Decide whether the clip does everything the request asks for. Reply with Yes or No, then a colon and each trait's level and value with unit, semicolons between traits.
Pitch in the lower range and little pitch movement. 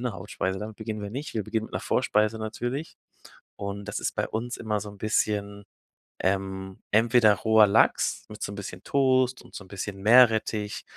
Yes: low, 105 Hz; narrow, 2.0 semitones